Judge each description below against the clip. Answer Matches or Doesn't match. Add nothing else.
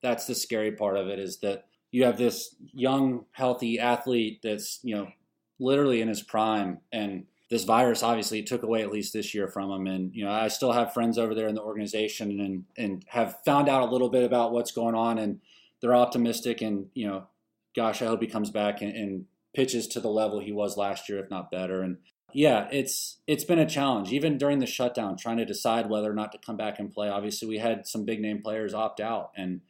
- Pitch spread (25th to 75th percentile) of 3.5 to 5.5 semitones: Doesn't match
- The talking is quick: Matches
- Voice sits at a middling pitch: Doesn't match